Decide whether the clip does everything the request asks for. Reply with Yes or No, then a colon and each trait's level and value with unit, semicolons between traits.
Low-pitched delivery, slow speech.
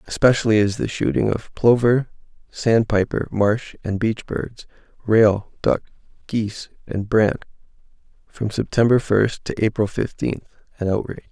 Yes: low, 110 Hz; slow, 125 wpm